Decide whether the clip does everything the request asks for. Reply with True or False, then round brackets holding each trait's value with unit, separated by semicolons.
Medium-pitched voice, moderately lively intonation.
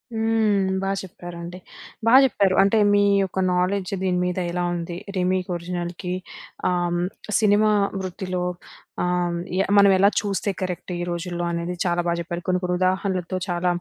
False (180 Hz; 1.8 semitones)